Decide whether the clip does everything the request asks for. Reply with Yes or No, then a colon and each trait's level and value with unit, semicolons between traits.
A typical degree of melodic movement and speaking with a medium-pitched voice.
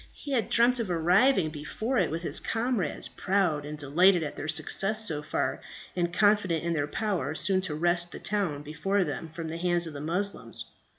Yes: average, 4.3 semitones; medium, 175 Hz